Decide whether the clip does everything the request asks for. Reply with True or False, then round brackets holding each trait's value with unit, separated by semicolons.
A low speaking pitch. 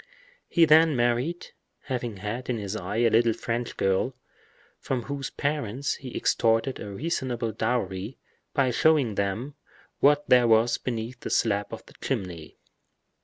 True (120 Hz)